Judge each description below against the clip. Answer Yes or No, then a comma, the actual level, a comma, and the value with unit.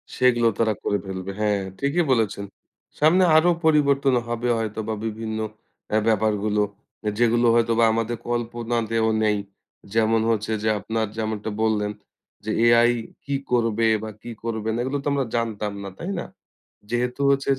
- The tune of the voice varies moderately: No, narrow, 1.8 semitones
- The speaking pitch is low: Yes, low, 115 Hz